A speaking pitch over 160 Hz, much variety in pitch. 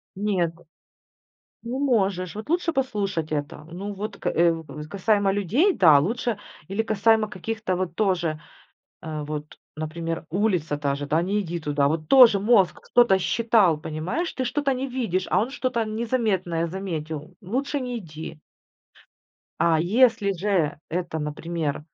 Yes: high, 190 Hz; wide, 5.7 semitones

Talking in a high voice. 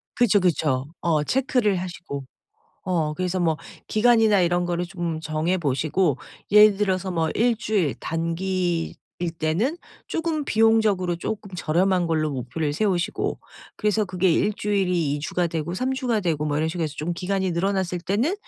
No: medium, 180 Hz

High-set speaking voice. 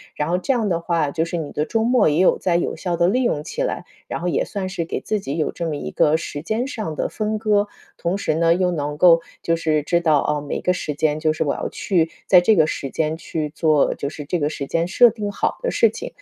No: medium, 170 Hz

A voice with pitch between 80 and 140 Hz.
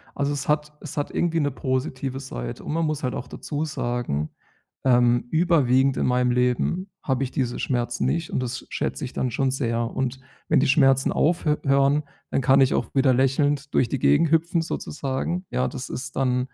Yes: low, 135 Hz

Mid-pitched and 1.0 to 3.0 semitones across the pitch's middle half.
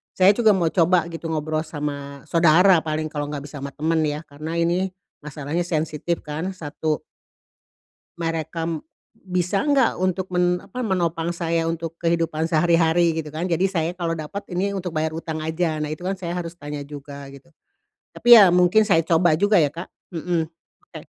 Yes: medium, 165 Hz; narrow, 2.4 semitones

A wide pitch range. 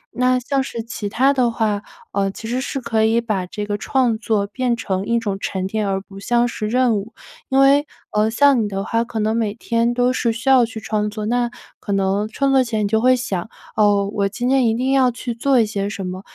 No: average, 3.2 semitones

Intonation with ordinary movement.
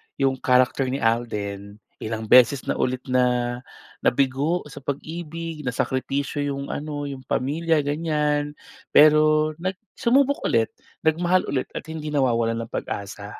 Yes: average, 3.7 semitones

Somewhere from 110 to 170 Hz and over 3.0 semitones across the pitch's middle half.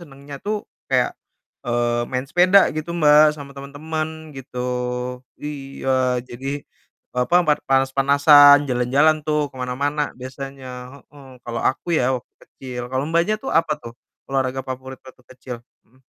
No: medium, 140 Hz; average, 2.7 semitones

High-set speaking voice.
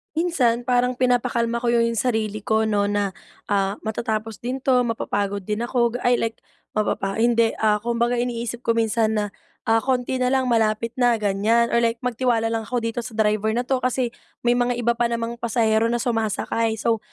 Yes: high, 230 Hz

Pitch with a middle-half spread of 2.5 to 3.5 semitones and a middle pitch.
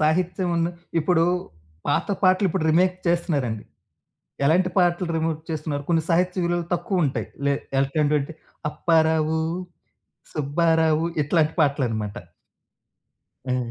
Yes: average, 3.1 semitones; medium, 160 Hz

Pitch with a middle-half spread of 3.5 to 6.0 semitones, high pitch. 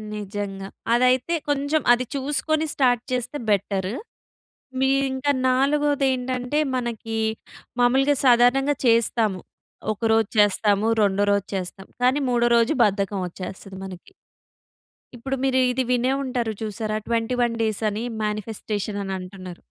Yes: average, 4.2 semitones; high, 235 Hz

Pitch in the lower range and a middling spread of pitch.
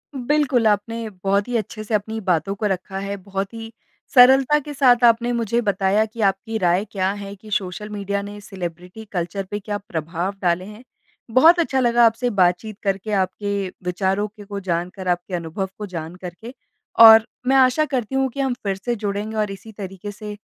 No: high, 205 Hz; average, 3.0 semitones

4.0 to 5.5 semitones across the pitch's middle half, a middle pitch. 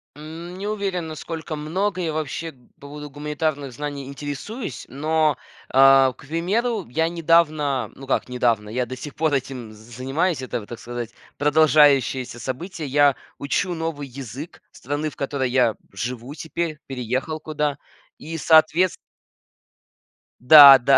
No: average, 3.6 semitones; medium, 145 Hz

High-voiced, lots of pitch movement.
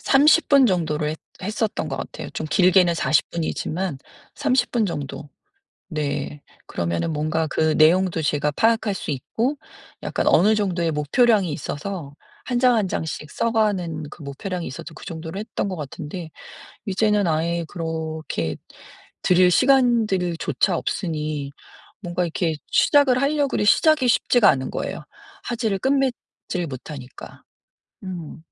No: medium, 175 Hz; wide, 5.8 semitones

